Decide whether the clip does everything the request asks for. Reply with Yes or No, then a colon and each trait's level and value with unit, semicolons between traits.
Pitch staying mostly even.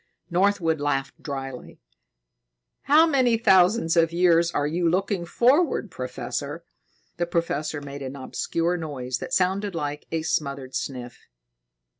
No: average, 4.8 semitones